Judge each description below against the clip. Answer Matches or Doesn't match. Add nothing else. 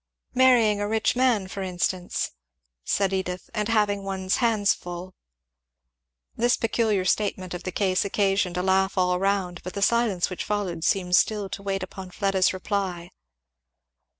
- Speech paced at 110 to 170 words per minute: Matches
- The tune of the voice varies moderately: Doesn't match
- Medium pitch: Doesn't match